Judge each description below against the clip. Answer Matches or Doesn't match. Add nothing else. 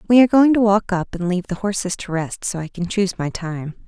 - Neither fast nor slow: Doesn't match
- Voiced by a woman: Matches